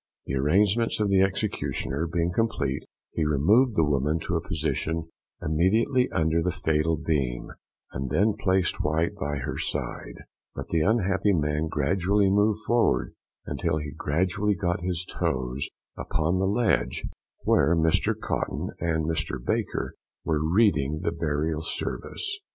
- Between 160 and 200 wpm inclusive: No, average, 140 wpm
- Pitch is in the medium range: No, very low, 80 Hz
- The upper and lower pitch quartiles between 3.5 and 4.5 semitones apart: Yes, average, 4.2 semitones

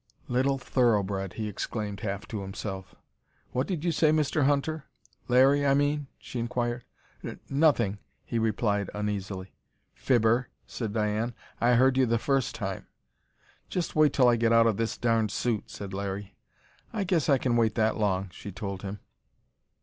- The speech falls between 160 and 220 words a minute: Yes, average, 165 wpm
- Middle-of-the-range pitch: No, low, 115 Hz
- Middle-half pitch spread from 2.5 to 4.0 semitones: No, average, 4.6 semitones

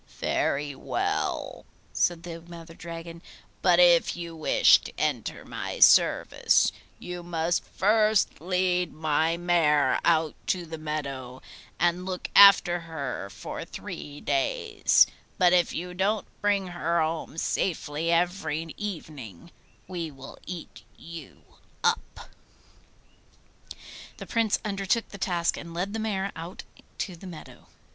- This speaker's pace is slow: Yes, slow, 125 wpm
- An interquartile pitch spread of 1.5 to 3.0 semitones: Yes, narrow, 2.4 semitones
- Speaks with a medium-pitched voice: Yes, medium, 170 Hz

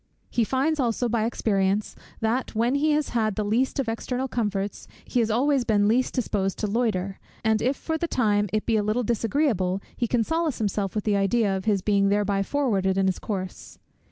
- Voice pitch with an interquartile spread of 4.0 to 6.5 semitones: No, average, 3.6 semitones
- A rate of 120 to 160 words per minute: No, fast, 205 wpm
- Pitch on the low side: No, high, 220 Hz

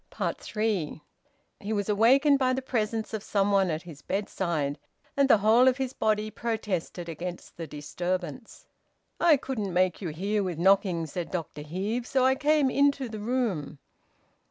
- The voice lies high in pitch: Yes, high, 205 Hz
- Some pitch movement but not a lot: No, wide, 5.8 semitones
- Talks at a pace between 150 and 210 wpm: Yes, average, 160 wpm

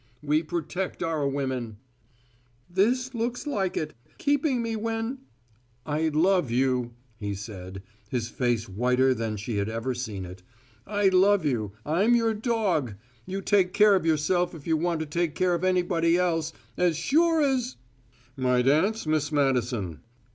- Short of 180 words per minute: Yes, average, 160 wpm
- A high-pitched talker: No, medium, 155 Hz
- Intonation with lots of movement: Yes, wide, 7.8 semitones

